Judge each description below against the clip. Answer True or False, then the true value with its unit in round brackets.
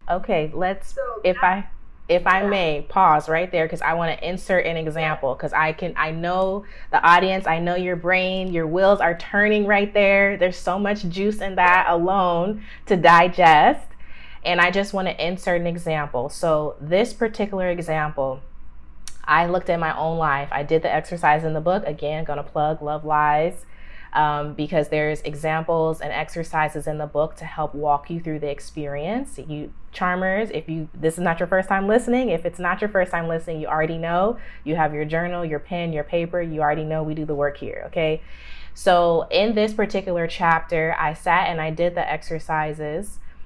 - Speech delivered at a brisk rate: False (195 wpm)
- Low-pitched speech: False (165 Hz)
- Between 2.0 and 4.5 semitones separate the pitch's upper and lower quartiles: True (3.1 semitones)